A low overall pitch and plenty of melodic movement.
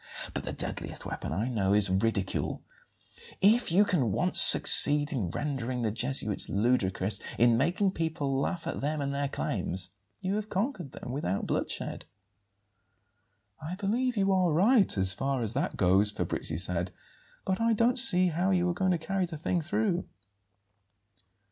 No: medium, 150 Hz; wide, 8.8 semitones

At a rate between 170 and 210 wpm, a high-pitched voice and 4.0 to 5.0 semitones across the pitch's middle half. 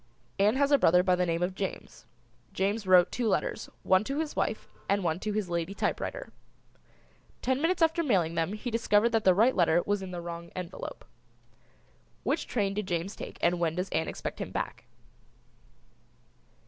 Yes: average, 185 wpm; high, 195 Hz; average, 4.3 semitones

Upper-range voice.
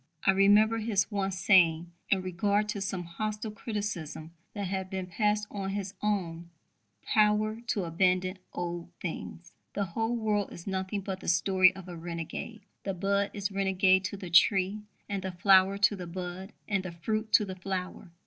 Yes: high, 195 Hz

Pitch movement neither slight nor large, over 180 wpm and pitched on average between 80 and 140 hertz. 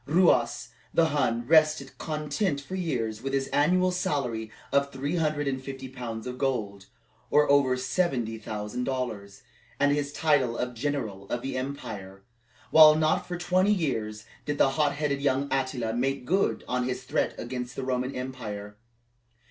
No: average, 3.6 semitones; average, 155 wpm; low, 135 Hz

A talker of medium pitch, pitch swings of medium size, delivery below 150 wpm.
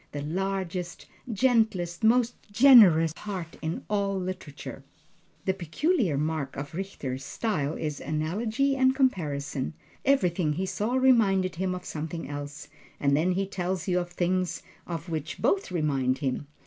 Yes: medium, 180 Hz; average, 4.4 semitones; average, 140 wpm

